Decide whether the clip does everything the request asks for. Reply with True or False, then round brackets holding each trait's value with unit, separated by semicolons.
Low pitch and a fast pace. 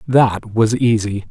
False (110 Hz; 140 wpm)